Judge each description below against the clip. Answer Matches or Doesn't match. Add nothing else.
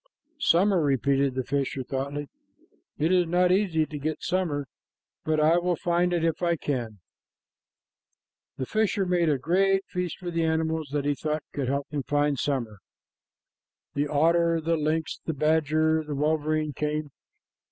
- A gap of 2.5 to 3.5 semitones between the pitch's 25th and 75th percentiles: Matches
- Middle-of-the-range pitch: Matches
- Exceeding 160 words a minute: Matches